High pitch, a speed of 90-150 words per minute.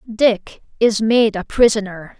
Yes: high, 215 Hz; slow, 135 wpm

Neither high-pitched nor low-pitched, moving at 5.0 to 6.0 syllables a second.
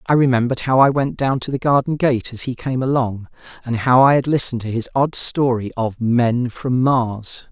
No: low, 125 Hz; 5.1 syllables/s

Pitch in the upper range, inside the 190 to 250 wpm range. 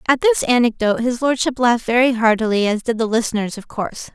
Yes: high, 235 Hz; fast, 205 wpm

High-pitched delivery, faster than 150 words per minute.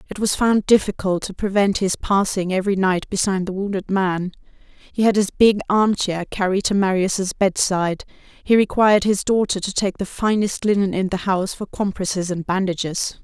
Yes: high, 195 Hz; average, 180 wpm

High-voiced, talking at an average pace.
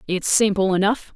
Yes: high, 195 Hz; average, 155 wpm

